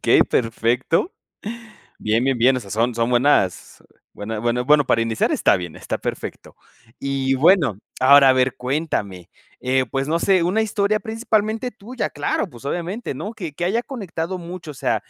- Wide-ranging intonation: Yes, wide, 7.5 semitones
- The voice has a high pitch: No, medium, 140 Hz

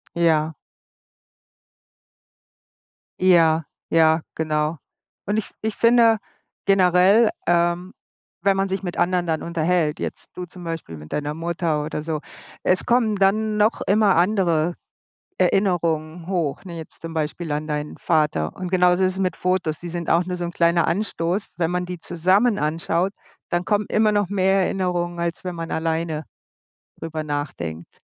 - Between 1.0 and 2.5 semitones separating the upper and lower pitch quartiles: No, average, 2.9 semitones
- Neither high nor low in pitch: Yes, medium, 175 Hz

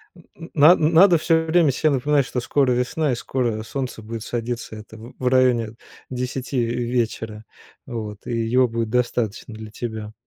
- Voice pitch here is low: Yes, low, 125 Hz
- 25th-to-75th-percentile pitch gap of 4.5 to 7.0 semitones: No, average, 3.3 semitones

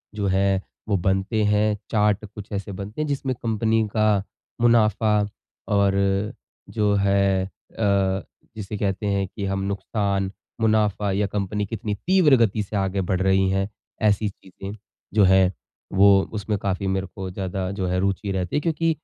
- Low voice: Yes, low, 100 Hz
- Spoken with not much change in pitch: Yes, narrow, 1.8 semitones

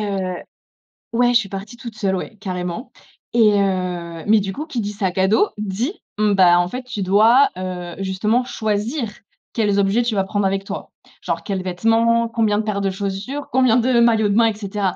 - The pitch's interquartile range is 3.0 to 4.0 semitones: Yes, average, 3.3 semitones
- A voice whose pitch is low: No, high, 210 Hz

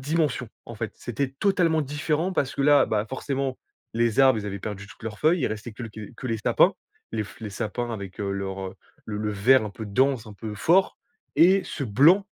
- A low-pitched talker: Yes, low, 120 Hz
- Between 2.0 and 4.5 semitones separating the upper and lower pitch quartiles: No, average, 5.3 semitones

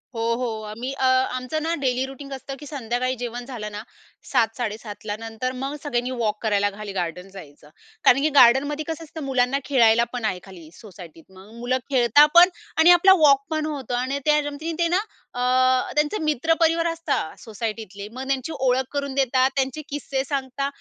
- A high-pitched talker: Yes, very high, 255 Hz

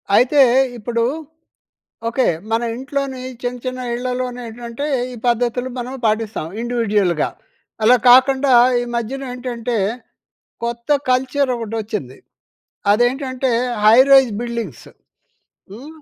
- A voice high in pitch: Yes, high, 245 Hz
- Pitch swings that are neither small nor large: No, narrow, 2.0 semitones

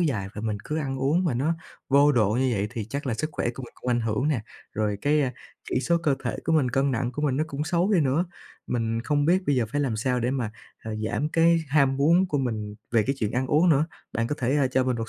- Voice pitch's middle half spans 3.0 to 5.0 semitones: Yes, average, 4.0 semitones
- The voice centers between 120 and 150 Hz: Yes, low, 135 Hz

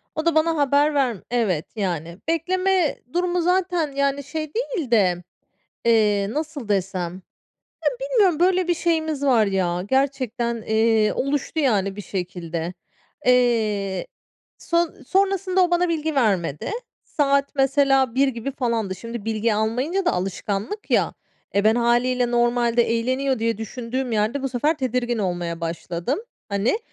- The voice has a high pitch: Yes, high, 245 Hz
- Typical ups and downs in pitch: No, wide, 6.4 semitones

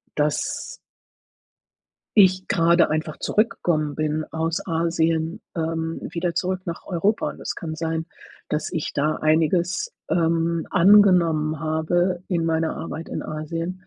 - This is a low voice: No, medium, 165 Hz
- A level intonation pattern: Yes, narrow, 1.8 semitones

